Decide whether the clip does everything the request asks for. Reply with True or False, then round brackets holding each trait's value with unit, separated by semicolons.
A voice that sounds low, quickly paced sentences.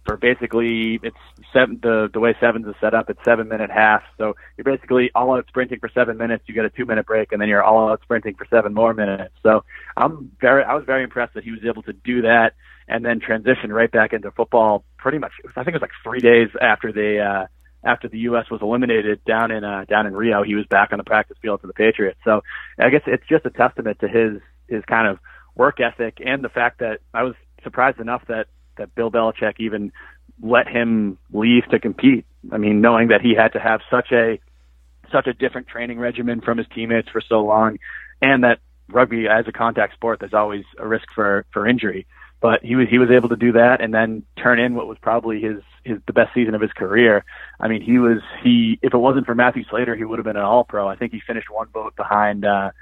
True (115 Hz; 240 wpm)